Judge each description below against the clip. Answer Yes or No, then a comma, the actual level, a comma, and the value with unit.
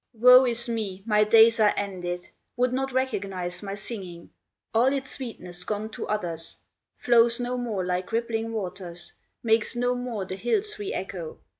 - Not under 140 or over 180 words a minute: Yes, average, 160 wpm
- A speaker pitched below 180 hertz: No, high, 225 Hz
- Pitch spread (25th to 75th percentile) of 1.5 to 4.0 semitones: No, average, 4.5 semitones